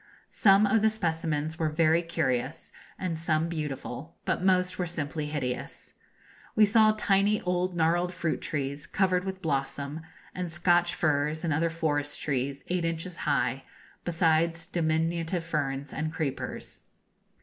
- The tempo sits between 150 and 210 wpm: No, average, 140 wpm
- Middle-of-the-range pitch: Yes, medium, 165 Hz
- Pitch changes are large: No, average, 3.0 semitones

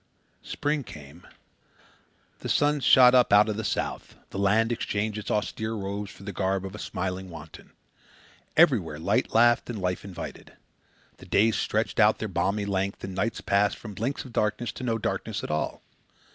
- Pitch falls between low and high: No, low, 105 Hz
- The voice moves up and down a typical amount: Yes, average, 3.0 semitones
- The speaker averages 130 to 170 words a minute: No, average, 180 wpm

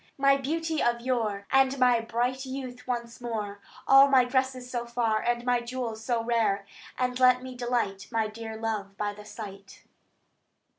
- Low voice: No, high, 240 Hz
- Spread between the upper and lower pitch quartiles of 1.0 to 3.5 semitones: Yes, narrow, 2.6 semitones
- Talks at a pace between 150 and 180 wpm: Yes, average, 165 wpm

